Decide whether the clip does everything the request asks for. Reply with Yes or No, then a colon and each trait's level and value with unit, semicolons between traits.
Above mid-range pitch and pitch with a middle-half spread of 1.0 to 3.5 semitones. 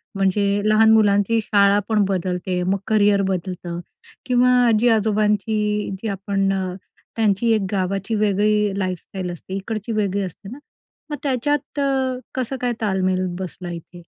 Yes: high, 205 Hz; narrow, 2.6 semitones